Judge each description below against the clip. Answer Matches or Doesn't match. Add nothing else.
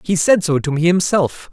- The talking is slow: Doesn't match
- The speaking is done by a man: Matches